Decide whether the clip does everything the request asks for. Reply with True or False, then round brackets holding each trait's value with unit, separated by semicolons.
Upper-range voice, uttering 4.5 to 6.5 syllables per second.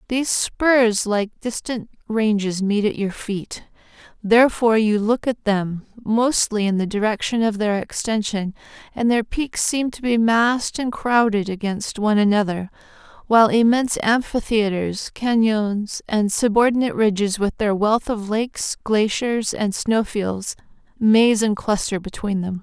False (215 Hz; 4.3 syllables/s)